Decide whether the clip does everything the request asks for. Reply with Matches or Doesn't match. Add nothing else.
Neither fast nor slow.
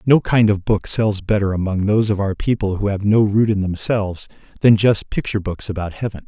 Doesn't match